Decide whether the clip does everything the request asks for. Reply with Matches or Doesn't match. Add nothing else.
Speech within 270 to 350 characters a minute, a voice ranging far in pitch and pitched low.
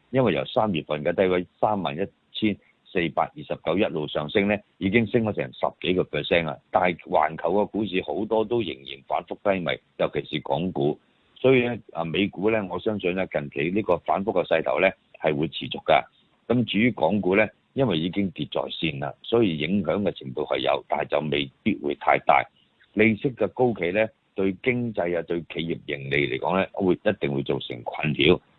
Matches